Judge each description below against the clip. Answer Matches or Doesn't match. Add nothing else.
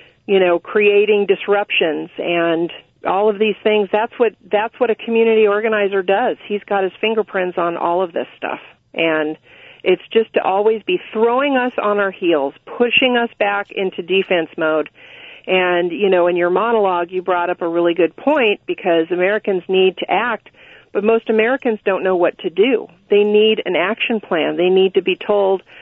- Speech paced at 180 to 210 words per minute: Matches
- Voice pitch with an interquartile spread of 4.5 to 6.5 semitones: Doesn't match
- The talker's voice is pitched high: Matches